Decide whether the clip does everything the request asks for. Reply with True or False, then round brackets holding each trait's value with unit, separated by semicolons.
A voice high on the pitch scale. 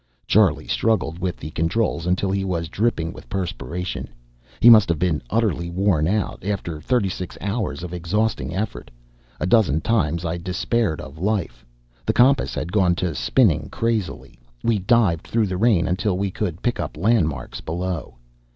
False (90 Hz)